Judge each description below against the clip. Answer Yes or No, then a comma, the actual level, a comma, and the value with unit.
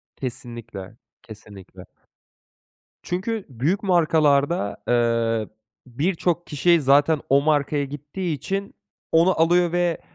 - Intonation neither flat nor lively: No, wide, 6.5 semitones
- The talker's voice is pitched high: No, medium, 145 Hz